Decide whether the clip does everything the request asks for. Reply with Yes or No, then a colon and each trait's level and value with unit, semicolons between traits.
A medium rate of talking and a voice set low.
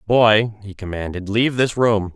Yes: average, 165 wpm; low, 105 Hz